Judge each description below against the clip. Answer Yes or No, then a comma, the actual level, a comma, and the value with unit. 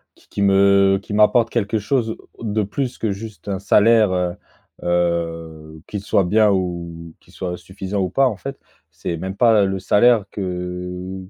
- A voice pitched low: Yes, very low, 95 Hz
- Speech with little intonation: No, average, 3.1 semitones